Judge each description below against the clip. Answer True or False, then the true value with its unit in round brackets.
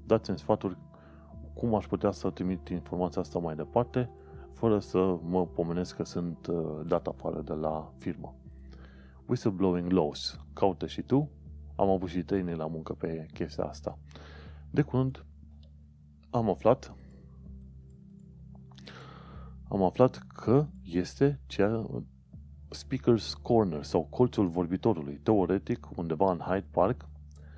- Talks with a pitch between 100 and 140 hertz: False (80 Hz)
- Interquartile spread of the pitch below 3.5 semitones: False (4.5 semitones)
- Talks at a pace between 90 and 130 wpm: True (120 wpm)